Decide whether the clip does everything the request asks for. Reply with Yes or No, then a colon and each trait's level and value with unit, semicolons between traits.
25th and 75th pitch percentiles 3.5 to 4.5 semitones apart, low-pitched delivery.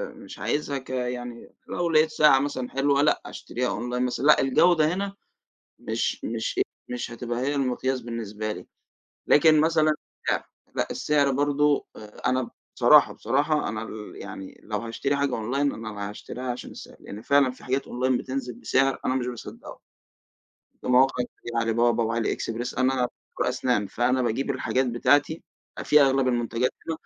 No: average, 3.1 semitones; low, 130 Hz